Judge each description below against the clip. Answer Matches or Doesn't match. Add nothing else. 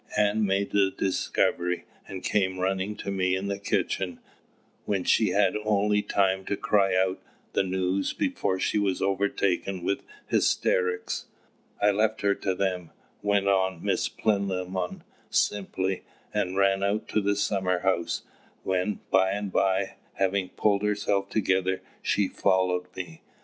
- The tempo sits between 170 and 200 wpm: Doesn't match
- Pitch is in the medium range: Doesn't match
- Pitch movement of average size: Doesn't match